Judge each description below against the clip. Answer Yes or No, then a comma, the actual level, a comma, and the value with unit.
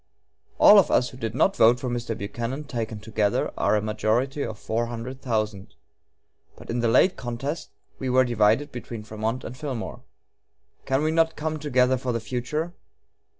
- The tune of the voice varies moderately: Yes, average, 3.2 semitones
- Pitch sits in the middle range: No, low, 120 Hz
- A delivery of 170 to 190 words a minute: Yes, average, 175 wpm